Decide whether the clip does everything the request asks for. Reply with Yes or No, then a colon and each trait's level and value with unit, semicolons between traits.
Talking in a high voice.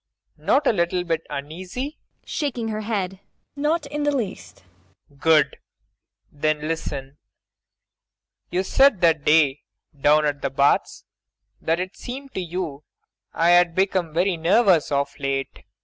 No: medium, 170 Hz